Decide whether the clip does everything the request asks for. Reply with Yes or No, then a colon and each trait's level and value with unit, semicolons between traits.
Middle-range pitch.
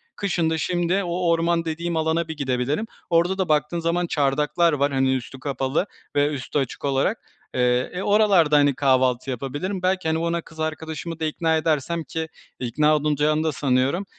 Yes: medium, 155 Hz